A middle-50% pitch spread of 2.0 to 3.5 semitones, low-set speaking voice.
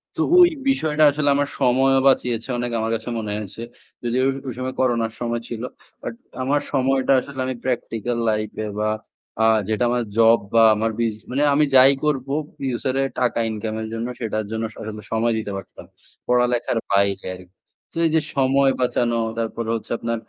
Yes: average, 2.8 semitones; low, 120 Hz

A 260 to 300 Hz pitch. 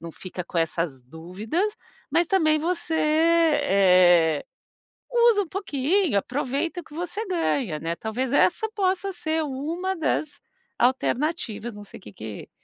Yes: very high, 290 Hz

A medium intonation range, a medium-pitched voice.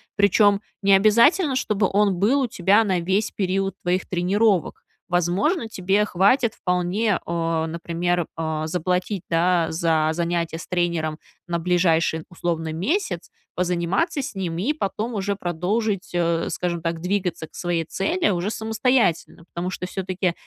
Yes: average, 3.3 semitones; medium, 180 Hz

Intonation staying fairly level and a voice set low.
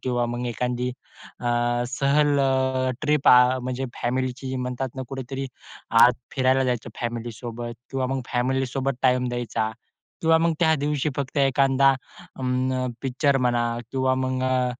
Yes: narrow, 1.5 semitones; low, 130 Hz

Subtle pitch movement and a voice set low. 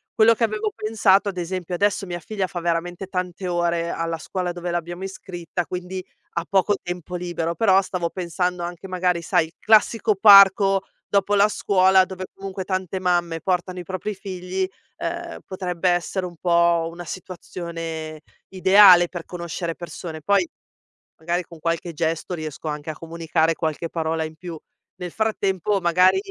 No: narrow, 2.1 semitones; medium, 180 Hz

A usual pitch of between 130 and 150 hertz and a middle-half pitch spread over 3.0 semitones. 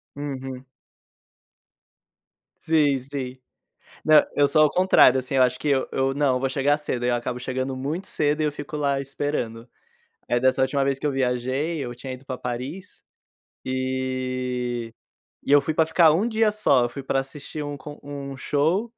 No: low, 135 Hz; narrow, 2.4 semitones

